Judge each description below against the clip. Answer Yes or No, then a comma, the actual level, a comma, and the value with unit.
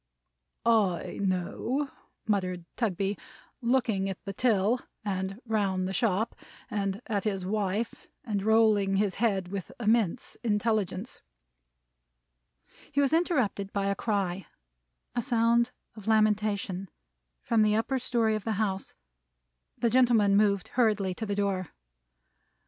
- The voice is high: Yes, high, 210 Hz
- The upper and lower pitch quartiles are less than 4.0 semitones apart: Yes, average, 2.8 semitones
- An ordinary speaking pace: No, slow, 125 wpm